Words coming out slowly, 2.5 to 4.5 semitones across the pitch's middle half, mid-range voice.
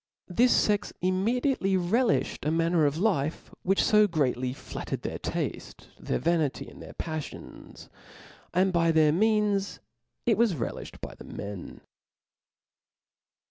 No: slow, 130 wpm; average, 5.2 semitones; medium, 180 Hz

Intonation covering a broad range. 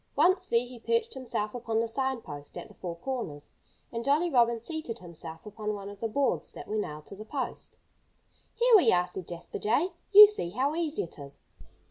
Yes: wide, 7.3 semitones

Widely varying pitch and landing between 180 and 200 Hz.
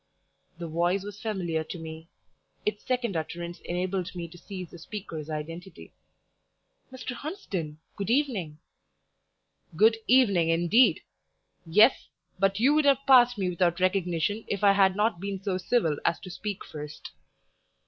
No: average, 4.2 semitones; high, 190 Hz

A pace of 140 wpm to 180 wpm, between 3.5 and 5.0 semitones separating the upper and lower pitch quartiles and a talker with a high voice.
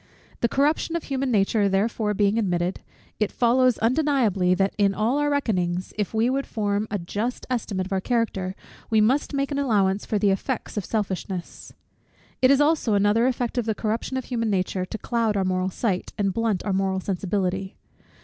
No: average, 190 wpm; average, 4.1 semitones; high, 215 Hz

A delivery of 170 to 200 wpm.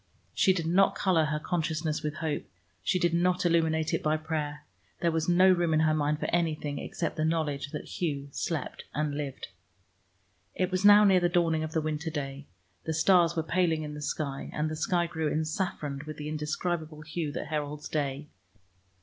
Yes: average, 190 wpm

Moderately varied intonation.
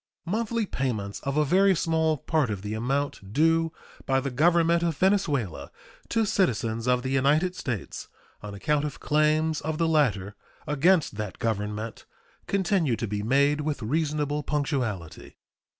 No: wide, 6.1 semitones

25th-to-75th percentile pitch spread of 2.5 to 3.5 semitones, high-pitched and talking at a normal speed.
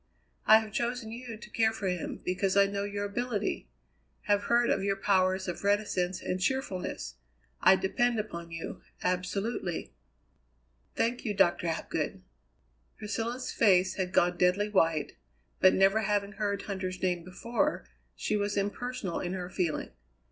Yes: average, 2.9 semitones; high, 200 Hz; average, 150 wpm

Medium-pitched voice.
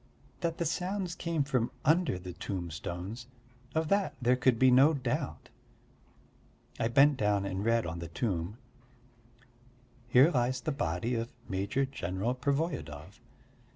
No: low, 125 Hz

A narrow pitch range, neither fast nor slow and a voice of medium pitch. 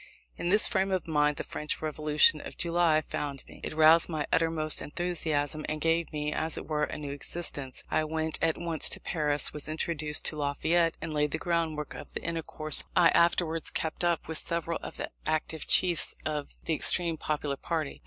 Yes: narrow, 1.8 semitones; average, 195 wpm; medium, 155 Hz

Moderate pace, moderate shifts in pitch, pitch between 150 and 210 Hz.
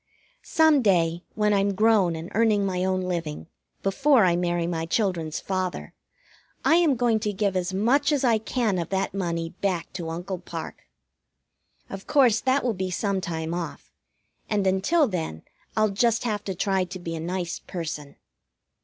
Yes: average, 170 wpm; average, 3.9 semitones; high, 190 Hz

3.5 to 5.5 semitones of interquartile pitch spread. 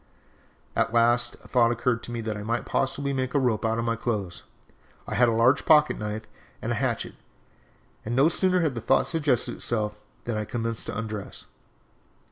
No: average, 2.8 semitones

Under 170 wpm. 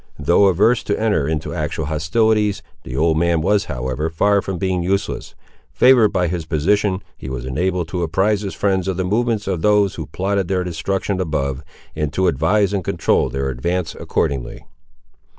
No: average, 175 wpm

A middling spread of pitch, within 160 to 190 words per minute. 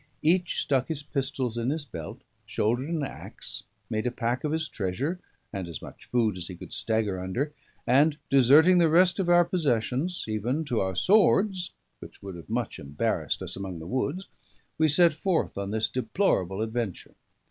No: wide, 6.9 semitones; average, 180 wpm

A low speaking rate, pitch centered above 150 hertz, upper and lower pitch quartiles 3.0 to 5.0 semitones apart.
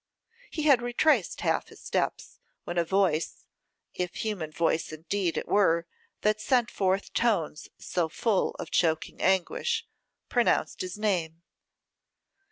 Yes: slow, 130 wpm; high, 190 Hz; average, 4.6 semitones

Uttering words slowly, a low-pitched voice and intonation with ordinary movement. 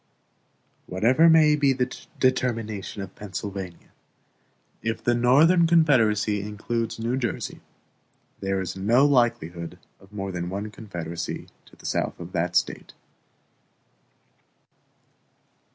Yes: slow, 110 wpm; low, 110 Hz; average, 4.8 semitones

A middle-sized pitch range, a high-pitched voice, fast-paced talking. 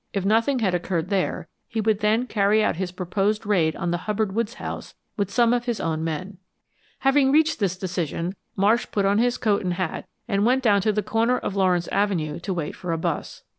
Yes: average, 3.7 semitones; high, 200 Hz; fast, 215 wpm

